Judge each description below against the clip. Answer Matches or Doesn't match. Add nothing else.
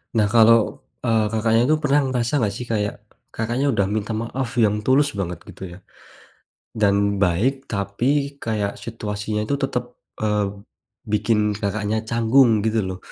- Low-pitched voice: Matches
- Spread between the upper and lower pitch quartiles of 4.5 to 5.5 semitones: Doesn't match